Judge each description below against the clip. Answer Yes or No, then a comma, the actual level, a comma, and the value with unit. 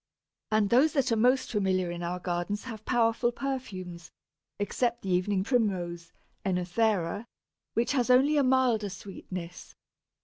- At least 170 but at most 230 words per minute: No, slow, 135 wpm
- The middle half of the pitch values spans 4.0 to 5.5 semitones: Yes, average, 5.2 semitones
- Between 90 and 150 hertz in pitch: No, high, 210 Hz